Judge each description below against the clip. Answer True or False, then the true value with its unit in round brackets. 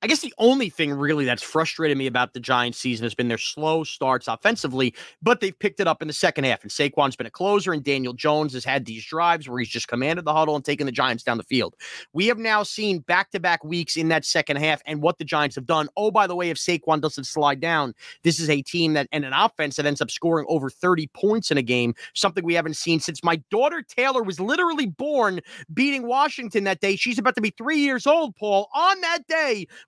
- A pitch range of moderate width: False (6.3 semitones)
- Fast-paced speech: True (250 wpm)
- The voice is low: False (160 Hz)